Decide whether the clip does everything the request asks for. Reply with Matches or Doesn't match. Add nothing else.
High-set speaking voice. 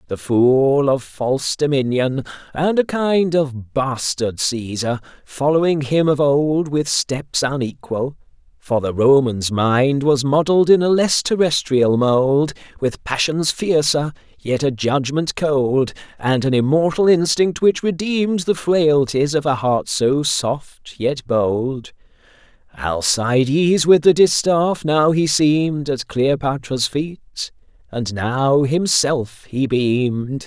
Doesn't match